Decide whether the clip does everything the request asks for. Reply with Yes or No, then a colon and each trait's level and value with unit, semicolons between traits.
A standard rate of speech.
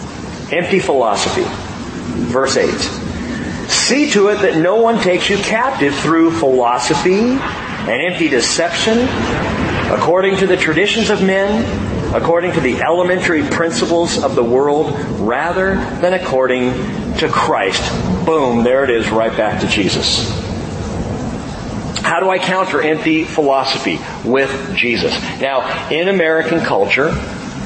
No: slow, 125 wpm